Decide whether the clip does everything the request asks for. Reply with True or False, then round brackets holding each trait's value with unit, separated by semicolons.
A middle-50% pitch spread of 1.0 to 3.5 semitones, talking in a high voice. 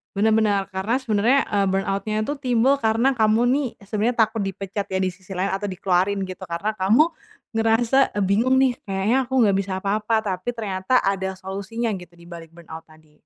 True (3.1 semitones; 200 Hz)